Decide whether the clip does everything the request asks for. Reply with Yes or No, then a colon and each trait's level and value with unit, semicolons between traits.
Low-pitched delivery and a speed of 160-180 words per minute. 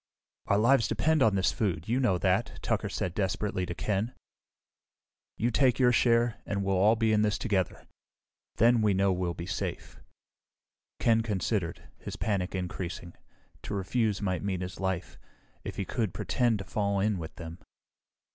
Yes: low, 100 Hz; average, 165 wpm